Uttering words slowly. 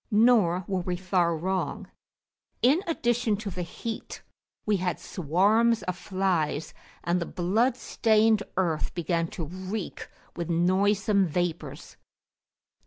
Yes: slow, 120 wpm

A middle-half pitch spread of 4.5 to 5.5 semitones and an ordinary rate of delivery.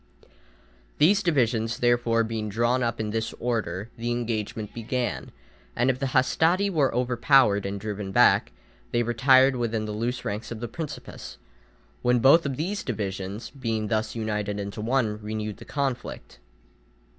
No: average, 3.1 semitones; average, 145 wpm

